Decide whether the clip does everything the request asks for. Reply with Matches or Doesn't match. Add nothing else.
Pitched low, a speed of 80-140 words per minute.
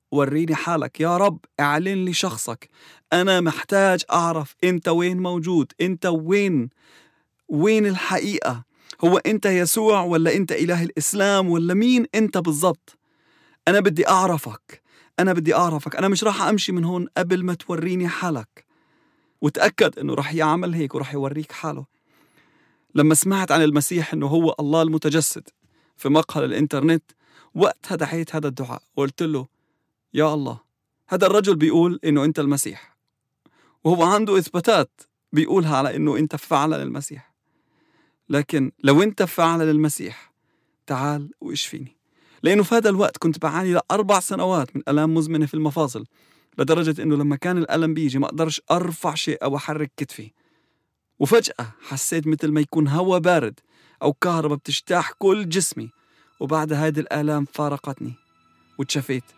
Doesn't match